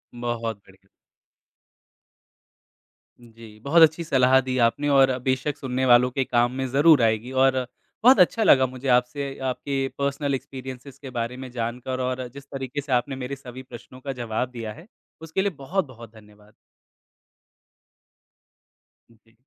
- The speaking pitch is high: No, low, 130 Hz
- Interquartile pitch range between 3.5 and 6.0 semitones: No, average, 2.7 semitones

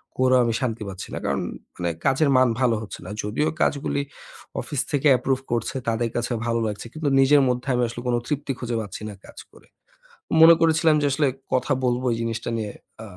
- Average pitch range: Yes, average, 3.5 semitones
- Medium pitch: No, low, 125 Hz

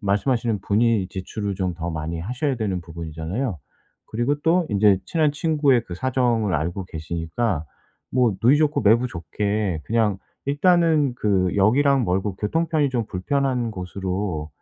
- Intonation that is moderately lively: No, wide, 6.1 semitones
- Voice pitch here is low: Yes, low, 105 Hz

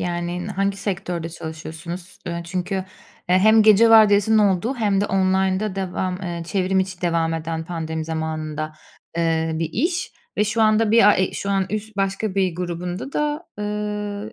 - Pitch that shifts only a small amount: No, average, 3.5 semitones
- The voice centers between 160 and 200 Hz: Yes, high, 190 Hz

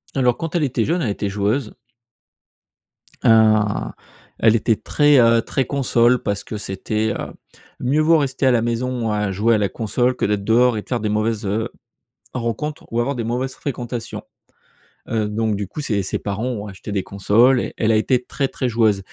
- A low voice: Yes, low, 115 Hz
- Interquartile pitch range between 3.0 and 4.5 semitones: Yes, average, 3.3 semitones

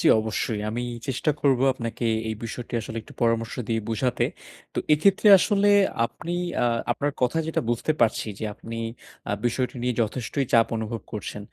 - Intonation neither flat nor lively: Yes, average, 3.2 semitones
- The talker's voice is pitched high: No, low, 120 Hz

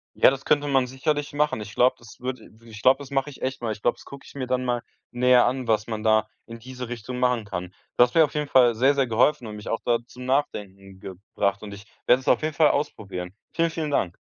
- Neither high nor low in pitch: No, low, 125 Hz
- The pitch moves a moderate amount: Yes, average, 3.8 semitones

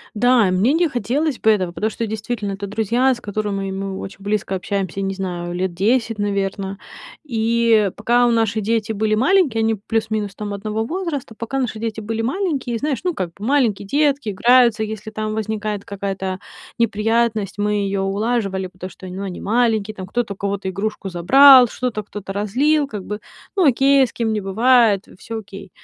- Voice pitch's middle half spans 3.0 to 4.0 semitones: Yes, average, 3.3 semitones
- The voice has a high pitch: Yes, high, 215 Hz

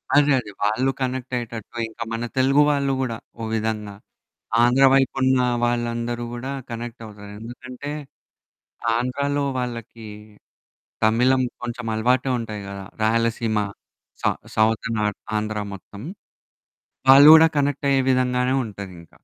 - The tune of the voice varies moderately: Yes, average, 3.0 semitones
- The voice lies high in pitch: No, low, 120 Hz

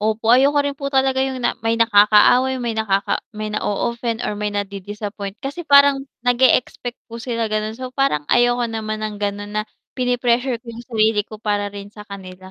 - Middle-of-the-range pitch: No, high, 225 Hz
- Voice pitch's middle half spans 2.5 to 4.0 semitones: Yes, average, 3.2 semitones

